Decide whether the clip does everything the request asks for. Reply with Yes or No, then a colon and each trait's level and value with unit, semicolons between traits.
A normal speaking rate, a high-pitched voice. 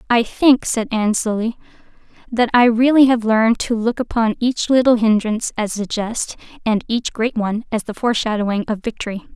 Yes: average, 180 wpm; high, 225 Hz